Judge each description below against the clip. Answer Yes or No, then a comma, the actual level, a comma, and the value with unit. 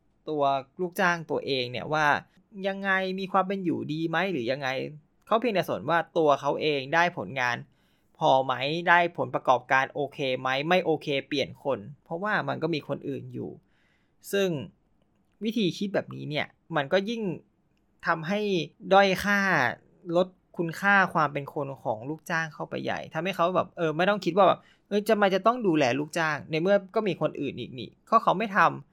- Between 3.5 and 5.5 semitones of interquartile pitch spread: Yes, average, 4.7 semitones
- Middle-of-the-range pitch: Yes, medium, 165 Hz